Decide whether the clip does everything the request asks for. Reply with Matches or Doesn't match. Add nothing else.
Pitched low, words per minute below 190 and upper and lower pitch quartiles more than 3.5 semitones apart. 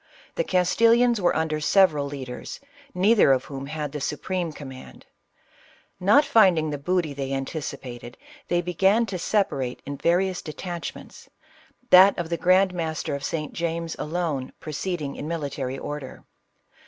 Doesn't match